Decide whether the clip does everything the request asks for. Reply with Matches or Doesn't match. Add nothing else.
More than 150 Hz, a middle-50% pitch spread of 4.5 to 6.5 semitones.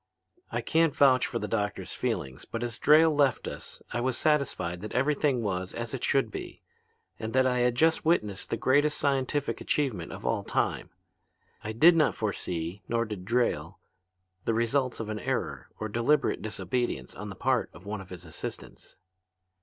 Doesn't match